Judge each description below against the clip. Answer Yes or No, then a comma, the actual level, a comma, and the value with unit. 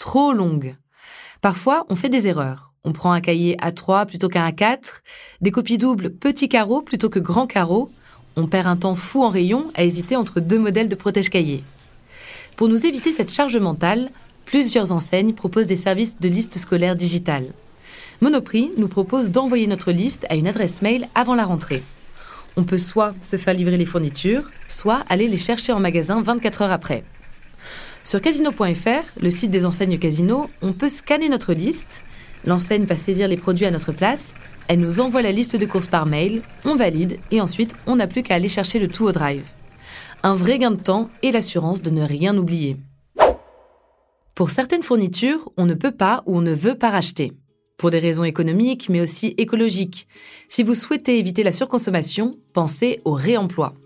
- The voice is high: Yes, high, 195 Hz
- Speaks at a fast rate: No, average, 185 wpm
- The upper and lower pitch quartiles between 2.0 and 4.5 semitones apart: No, wide, 5.5 semitones